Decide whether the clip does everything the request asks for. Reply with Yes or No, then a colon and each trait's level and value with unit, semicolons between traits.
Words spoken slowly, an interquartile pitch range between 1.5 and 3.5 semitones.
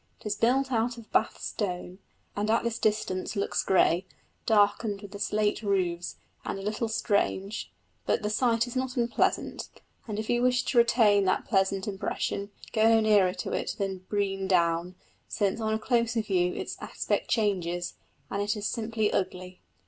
No: average, 170 wpm; average, 2.8 semitones